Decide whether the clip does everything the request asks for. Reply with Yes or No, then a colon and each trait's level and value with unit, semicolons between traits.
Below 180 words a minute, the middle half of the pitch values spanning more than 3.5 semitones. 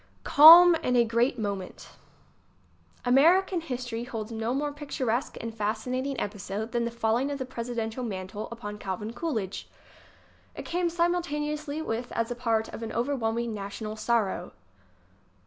Yes: average, 145 wpm; average, 4.2 semitones